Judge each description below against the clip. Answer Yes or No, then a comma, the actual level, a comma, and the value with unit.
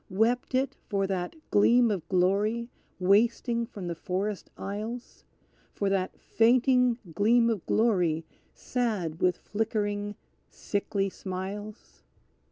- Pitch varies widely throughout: No, average, 3.6 semitones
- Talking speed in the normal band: No, slow, 110 wpm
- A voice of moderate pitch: No, high, 205 Hz